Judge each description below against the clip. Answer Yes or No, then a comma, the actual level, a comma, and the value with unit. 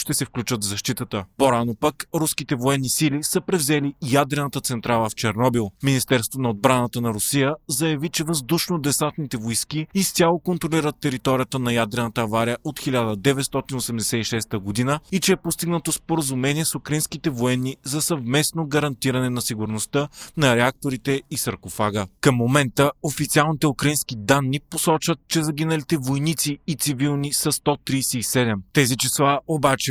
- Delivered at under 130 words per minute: No, average, 135 wpm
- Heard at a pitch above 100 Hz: Yes, medium, 140 Hz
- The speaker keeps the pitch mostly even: No, average, 3.9 semitones